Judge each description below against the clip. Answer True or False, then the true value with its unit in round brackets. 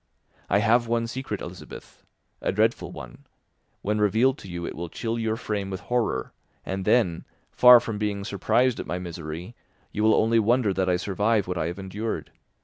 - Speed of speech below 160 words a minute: False (185 wpm)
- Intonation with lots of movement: False (3.9 semitones)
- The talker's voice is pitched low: True (105 Hz)